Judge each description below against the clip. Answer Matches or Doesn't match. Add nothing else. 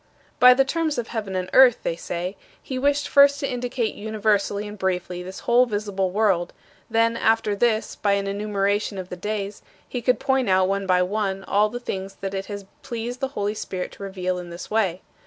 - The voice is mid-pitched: Doesn't match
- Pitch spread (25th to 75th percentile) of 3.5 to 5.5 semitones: Matches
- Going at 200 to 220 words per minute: Matches